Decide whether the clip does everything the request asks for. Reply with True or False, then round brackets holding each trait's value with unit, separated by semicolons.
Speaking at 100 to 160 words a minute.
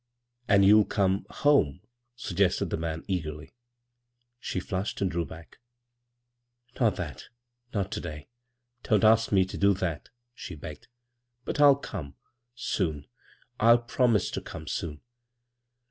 True (155 wpm)